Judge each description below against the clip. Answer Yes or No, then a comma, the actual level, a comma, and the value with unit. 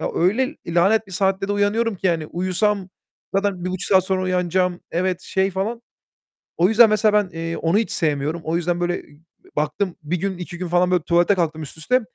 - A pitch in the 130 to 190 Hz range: Yes, medium, 185 Hz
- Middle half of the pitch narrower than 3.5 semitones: Yes, average, 2.7 semitones